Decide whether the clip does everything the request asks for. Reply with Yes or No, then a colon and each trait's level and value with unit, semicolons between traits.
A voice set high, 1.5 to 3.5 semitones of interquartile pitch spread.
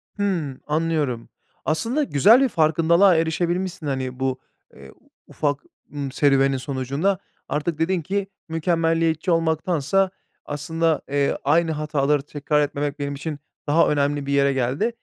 No: medium, 155 Hz; average, 2.9 semitones